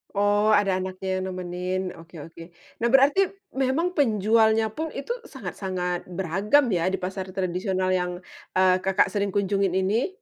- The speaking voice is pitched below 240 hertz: Yes, high, 190 Hz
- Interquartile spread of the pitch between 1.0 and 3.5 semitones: Yes, average, 2.9 semitones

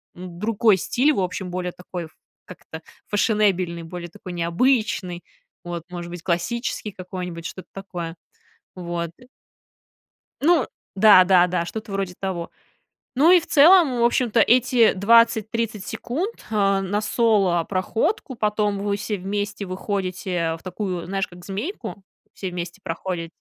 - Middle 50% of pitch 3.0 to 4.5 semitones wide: Yes, average, 3.8 semitones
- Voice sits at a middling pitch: No, high, 195 Hz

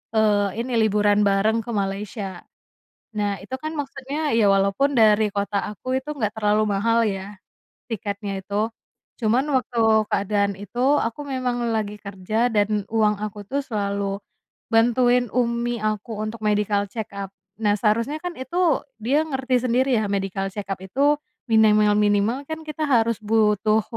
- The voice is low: No, high, 215 Hz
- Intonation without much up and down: No, average, 3.4 semitones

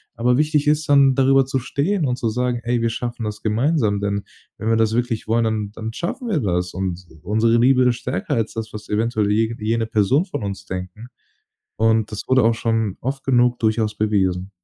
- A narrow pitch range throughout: No, average, 3.0 semitones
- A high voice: No, low, 115 Hz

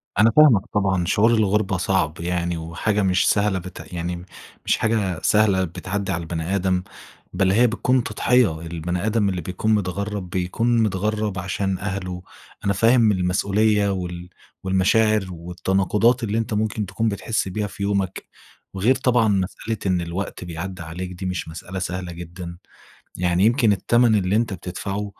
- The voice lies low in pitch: Yes, very low, 95 Hz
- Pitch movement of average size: Yes, average, 3.0 semitones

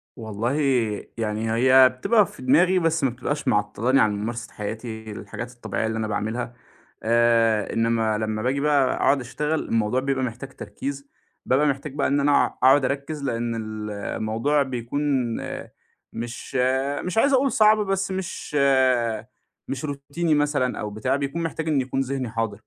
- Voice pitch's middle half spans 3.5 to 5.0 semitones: Yes, average, 4.2 semitones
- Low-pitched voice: Yes, low, 130 Hz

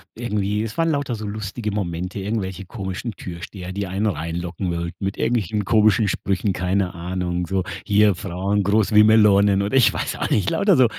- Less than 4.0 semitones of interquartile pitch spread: Yes, average, 2.8 semitones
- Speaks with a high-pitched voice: No, low, 100 Hz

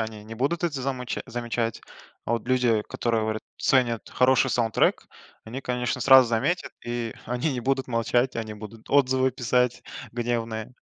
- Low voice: Yes, low, 120 Hz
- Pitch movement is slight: Yes, narrow, 2.3 semitones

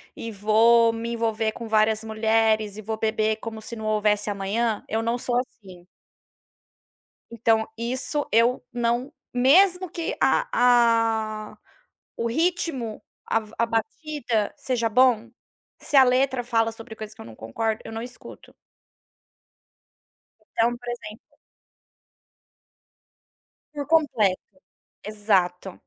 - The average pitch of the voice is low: No, high, 225 Hz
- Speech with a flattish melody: Yes, narrow, 2.2 semitones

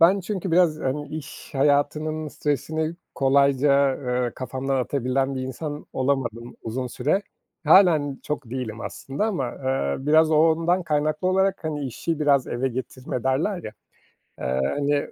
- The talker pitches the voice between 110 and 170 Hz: Yes, medium, 140 Hz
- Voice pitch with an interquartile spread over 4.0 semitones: No, average, 3.2 semitones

